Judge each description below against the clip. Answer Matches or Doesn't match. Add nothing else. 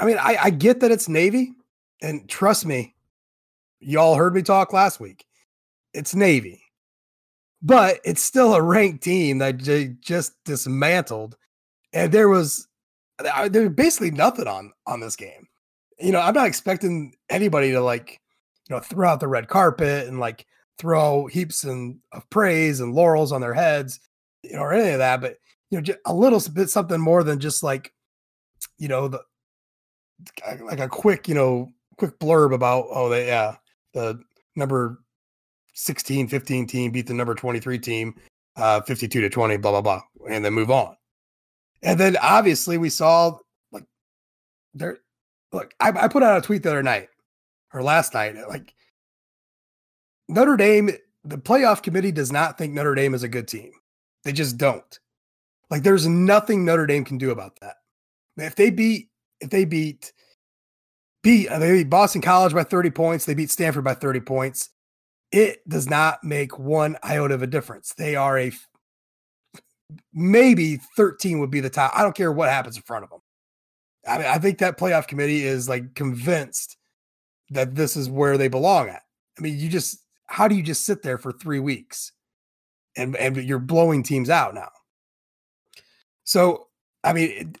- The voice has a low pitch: Doesn't match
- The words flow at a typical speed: Matches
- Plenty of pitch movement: Matches